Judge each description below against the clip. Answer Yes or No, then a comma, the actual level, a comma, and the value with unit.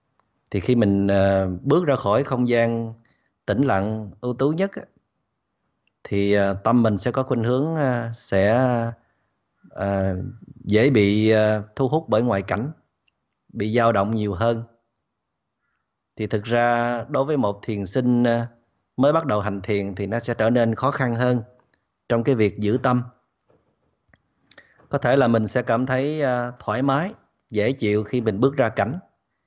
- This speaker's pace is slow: Yes, slow, 155 wpm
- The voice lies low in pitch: Yes, low, 115 Hz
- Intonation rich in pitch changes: No, average, 3.3 semitones